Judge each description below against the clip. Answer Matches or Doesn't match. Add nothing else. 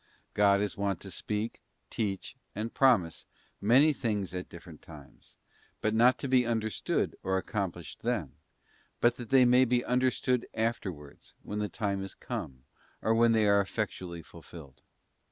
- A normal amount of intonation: Matches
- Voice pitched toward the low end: Matches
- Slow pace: Doesn't match